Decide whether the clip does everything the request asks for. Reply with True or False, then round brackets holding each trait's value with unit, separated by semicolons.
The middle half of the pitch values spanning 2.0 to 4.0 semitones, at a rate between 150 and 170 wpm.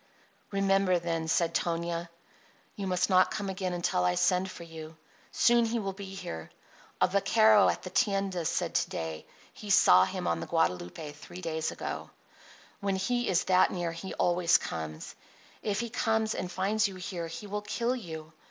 False (3.2 semitones; 180 wpm)